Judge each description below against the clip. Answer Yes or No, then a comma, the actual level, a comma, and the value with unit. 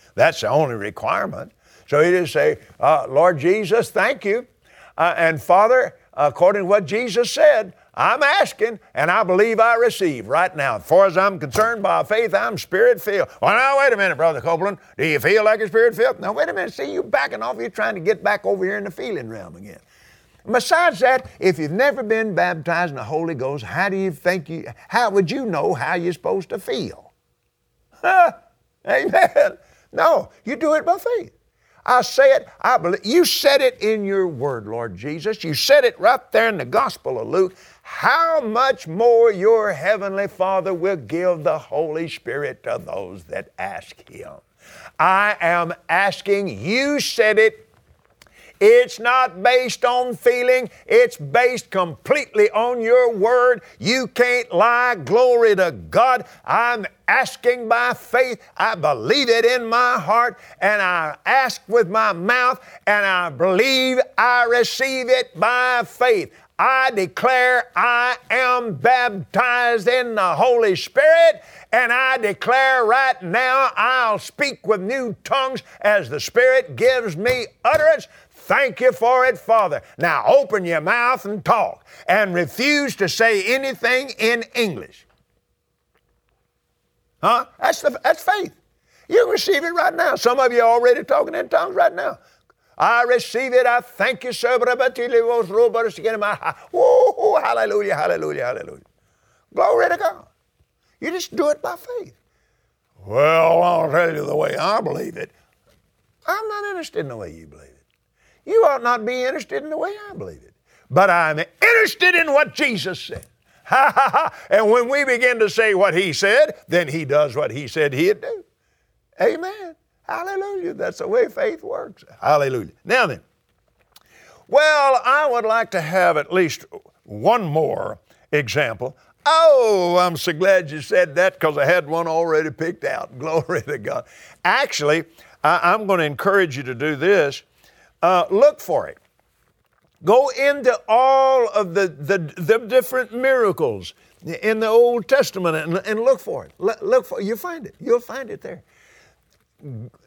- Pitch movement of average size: No, wide, 7.0 semitones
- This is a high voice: Yes, high, 240 Hz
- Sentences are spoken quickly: No, average, 165 wpm